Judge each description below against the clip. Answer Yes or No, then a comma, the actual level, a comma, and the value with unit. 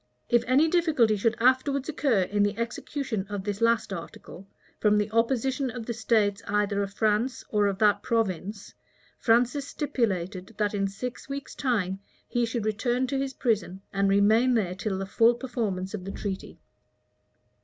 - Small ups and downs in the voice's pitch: No, average, 3.7 semitones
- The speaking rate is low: No, average, 165 wpm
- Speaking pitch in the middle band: No, high, 220 Hz